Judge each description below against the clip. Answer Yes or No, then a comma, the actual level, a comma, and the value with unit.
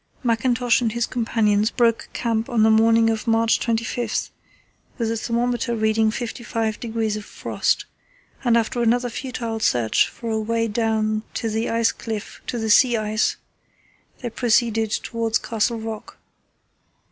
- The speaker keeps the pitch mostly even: Yes, narrow, 1.4 semitones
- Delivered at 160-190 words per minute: No, average, 140 wpm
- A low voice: No, high, 225 Hz